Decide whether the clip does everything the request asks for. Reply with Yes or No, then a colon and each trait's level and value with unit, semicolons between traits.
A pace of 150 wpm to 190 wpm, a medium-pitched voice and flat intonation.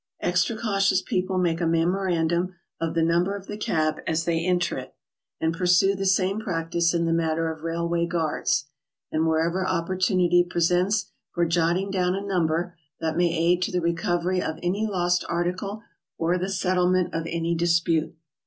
Yes: average, 170 wpm; medium, 175 Hz; narrow, 1.8 semitones